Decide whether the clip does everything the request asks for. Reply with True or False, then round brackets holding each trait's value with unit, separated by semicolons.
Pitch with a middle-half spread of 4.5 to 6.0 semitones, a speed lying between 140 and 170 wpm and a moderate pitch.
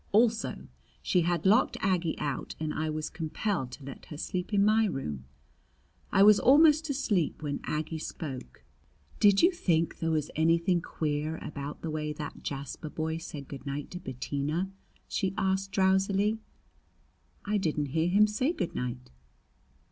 True (4.9 semitones; 155 wpm; 165 Hz)